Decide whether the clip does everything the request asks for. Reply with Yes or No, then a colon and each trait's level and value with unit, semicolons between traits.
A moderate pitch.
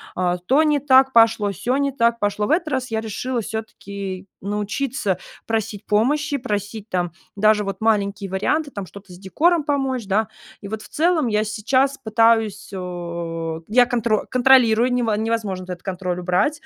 No: high, 220 Hz